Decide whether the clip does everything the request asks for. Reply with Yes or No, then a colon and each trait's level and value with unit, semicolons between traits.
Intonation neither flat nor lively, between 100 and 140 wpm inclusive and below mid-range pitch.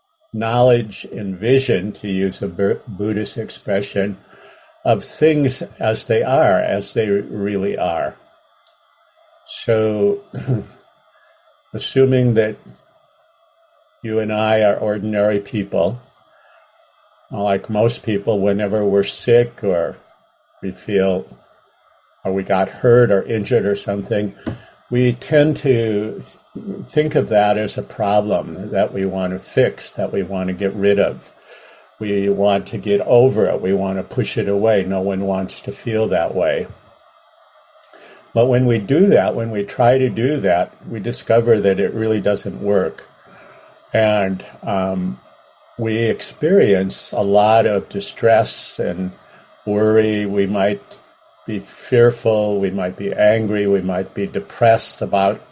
No: narrow, 2.3 semitones; slow, 135 wpm; low, 105 Hz